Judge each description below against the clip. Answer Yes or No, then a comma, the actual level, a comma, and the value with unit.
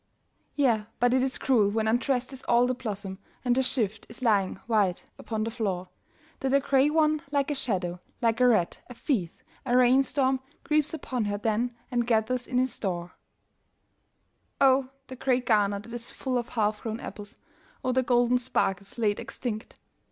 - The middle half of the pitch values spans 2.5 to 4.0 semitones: Yes, average, 3.4 semitones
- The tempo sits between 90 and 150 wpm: No, average, 180 wpm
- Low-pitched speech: No, high, 240 Hz